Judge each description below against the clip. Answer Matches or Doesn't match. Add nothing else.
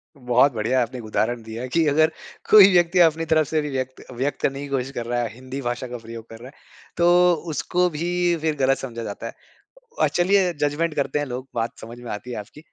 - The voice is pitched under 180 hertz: Matches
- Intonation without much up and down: Doesn't match